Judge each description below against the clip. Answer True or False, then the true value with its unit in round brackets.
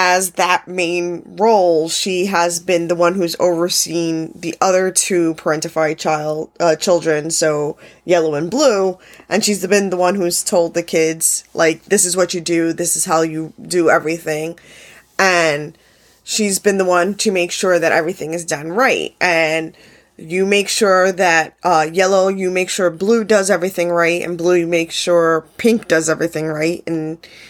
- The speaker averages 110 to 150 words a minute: False (175 wpm)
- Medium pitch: True (175 Hz)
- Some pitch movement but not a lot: False (2.3 semitones)